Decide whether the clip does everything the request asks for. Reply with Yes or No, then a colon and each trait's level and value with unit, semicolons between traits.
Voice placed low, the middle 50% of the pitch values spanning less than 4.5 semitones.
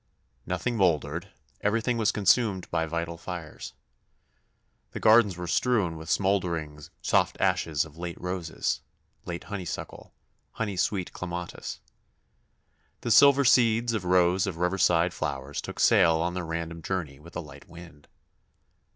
Yes: very low, 90 Hz; average, 3.6 semitones